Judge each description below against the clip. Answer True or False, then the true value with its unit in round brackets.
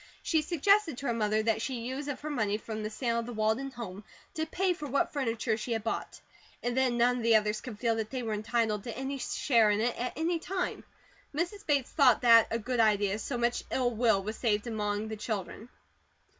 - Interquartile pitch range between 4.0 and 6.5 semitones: False (3.6 semitones)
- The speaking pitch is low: False (235 Hz)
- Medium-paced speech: False (225 wpm)